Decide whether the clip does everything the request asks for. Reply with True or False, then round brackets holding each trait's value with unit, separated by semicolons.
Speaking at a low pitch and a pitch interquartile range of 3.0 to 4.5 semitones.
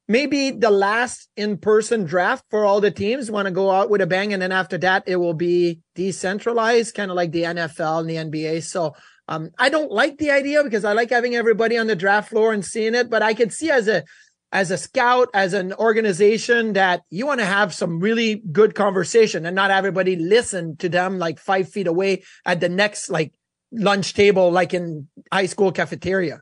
False (200 Hz; 3.7 semitones)